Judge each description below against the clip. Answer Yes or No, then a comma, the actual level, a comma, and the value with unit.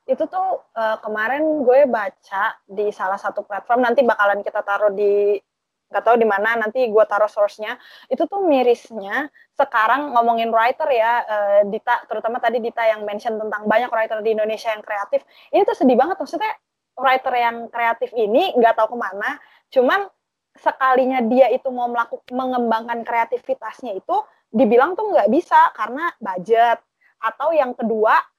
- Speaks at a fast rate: Yes, fast, 155 wpm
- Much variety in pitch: No, average, 3.4 semitones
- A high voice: Yes, high, 235 Hz